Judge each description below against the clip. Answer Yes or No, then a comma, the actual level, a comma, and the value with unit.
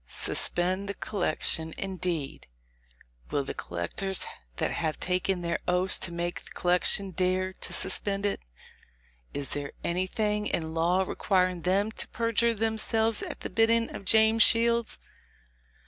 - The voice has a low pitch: No, medium, 185 Hz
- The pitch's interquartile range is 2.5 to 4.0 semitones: Yes, average, 3.7 semitones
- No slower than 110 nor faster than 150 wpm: Yes, slow, 135 wpm